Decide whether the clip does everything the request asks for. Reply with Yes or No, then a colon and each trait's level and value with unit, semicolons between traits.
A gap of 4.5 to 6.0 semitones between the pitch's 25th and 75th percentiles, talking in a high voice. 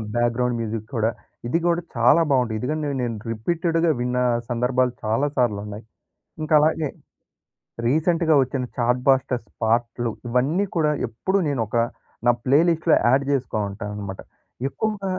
No: average, 5.0 semitones; low, 125 Hz